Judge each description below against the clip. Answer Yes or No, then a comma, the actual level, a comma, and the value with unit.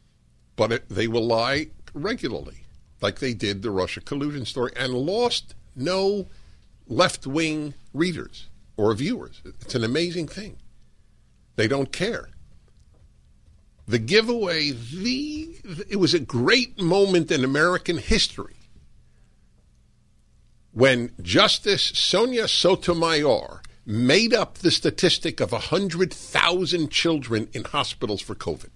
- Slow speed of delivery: Yes, slow, 115 wpm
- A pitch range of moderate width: No, wide, 7.4 semitones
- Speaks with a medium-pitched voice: Yes, medium, 150 Hz